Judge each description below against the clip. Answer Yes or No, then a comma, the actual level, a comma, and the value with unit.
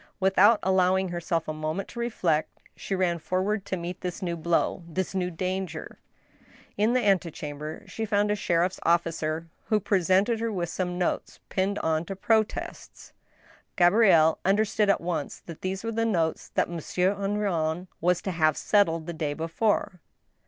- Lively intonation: No, average, 3.2 semitones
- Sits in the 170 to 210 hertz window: Yes, medium, 185 Hz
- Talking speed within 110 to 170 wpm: Yes, average, 165 wpm